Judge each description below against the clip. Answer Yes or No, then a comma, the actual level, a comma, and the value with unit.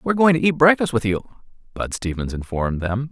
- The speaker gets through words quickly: Yes, fast, 210 wpm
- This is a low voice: Yes, low, 125 Hz